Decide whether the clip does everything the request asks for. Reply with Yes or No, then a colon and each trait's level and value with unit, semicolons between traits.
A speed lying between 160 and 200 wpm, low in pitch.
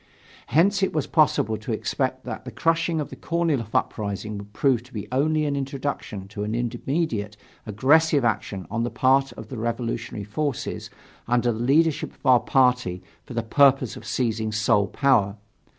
Yes: average, 170 wpm; low, 125 Hz